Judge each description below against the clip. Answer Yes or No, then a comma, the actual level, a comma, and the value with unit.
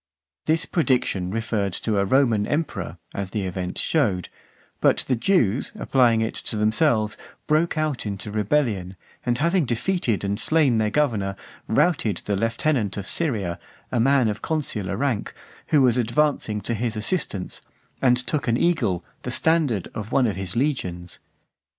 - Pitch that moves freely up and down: Yes, wide, 6.0 semitones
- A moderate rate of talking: Yes, average, 155 wpm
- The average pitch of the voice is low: Yes, low, 115 Hz